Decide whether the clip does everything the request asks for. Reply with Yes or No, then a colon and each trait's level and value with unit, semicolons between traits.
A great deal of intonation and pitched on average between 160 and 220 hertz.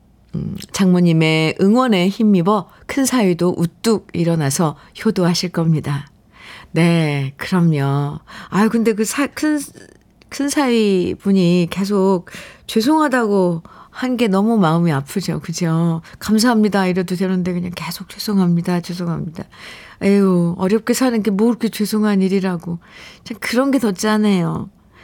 No: average, 4.3 semitones; high, 190 Hz